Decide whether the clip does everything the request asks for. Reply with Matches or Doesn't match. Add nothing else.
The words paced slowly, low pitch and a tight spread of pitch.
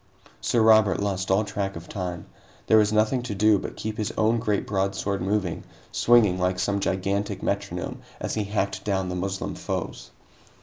Doesn't match